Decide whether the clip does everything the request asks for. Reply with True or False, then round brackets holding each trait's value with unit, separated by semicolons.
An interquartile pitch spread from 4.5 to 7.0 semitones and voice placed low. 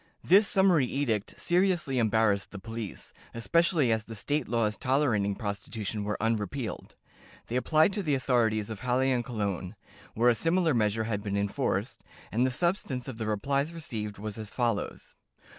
True (4.8 semitones; 115 Hz)